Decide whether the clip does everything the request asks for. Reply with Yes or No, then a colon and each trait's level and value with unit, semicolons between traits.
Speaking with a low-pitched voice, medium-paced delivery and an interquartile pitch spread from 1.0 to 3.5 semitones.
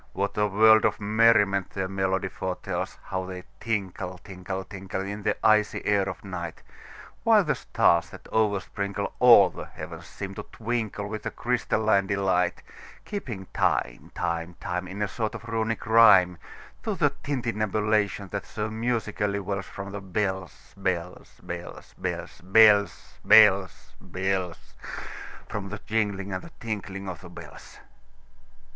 No: low, 100 Hz; slow, 120 wpm; narrow, 2.4 semitones